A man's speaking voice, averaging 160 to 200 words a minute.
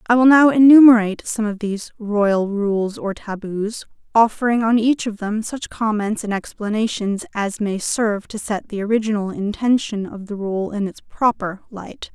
No: female; average, 175 wpm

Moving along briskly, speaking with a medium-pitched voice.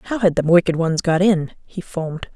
Yes: fast, 230 wpm; medium, 175 Hz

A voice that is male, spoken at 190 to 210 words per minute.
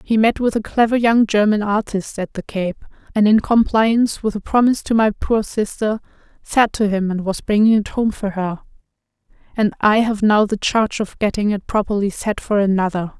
No: female; average, 200 wpm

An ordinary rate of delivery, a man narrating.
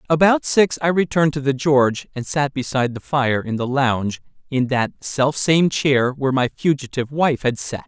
Yes: average, 185 wpm; male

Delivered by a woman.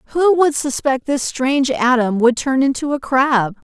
Yes: female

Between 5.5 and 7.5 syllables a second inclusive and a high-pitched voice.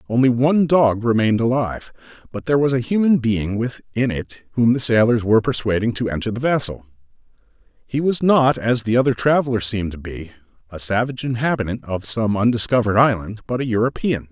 No: 6.0 syllables/s; low, 115 Hz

